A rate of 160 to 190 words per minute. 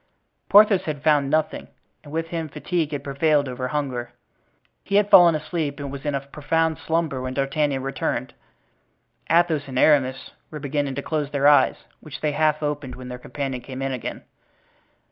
Yes: average, 175 wpm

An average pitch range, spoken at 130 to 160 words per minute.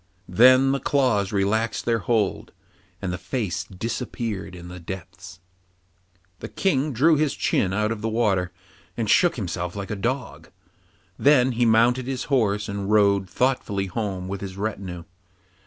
Yes: average, 4.5 semitones; average, 155 wpm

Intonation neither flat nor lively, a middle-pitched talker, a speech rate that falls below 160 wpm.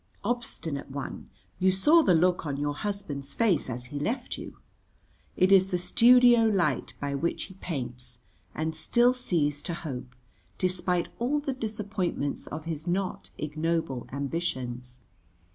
No: wide, 5.9 semitones; medium, 170 Hz; average, 145 wpm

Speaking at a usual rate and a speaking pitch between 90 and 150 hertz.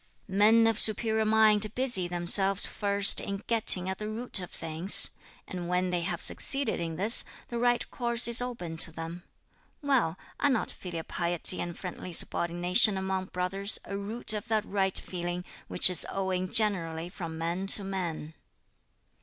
No: average, 160 wpm; high, 190 Hz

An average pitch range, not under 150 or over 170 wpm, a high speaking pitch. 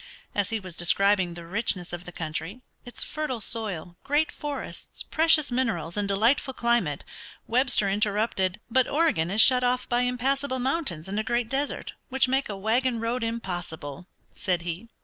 No: wide, 5.7 semitones; average, 165 wpm; high, 225 Hz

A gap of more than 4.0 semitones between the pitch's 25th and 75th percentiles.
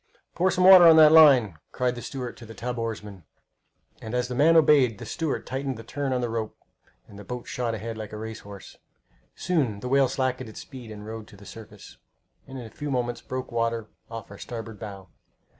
No: average, 3.4 semitones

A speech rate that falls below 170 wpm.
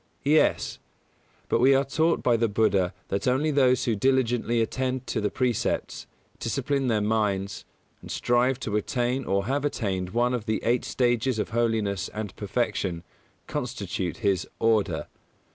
Yes: average, 150 wpm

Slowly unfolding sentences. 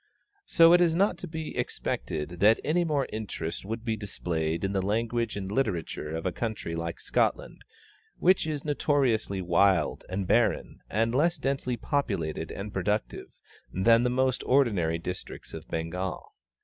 No: average, 155 wpm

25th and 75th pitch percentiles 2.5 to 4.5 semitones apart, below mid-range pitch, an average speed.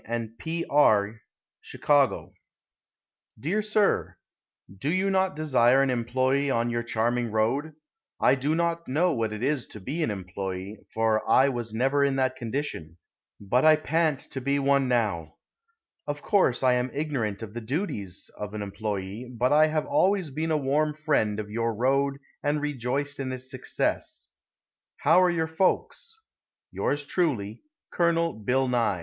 No: average, 5.2 semitones; low, 130 Hz; average, 160 wpm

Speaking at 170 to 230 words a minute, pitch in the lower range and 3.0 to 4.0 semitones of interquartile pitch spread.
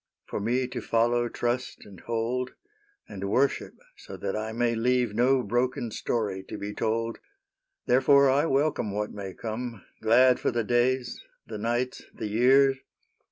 No: average, 180 wpm; low, 120 Hz; narrow, 2.6 semitones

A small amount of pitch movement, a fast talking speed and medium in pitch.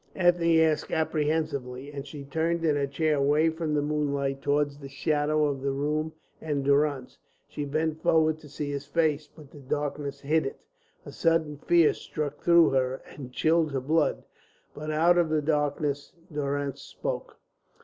No: narrow, 2.0 semitones; average, 170 wpm; medium, 150 Hz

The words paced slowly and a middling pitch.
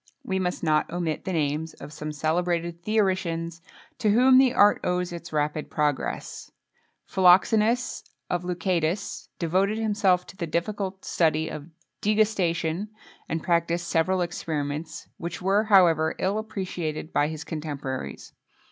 Yes: slow, 130 wpm; medium, 175 Hz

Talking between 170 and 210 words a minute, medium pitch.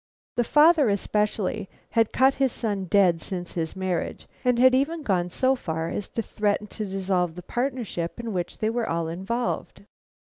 No: average, 175 wpm; high, 205 Hz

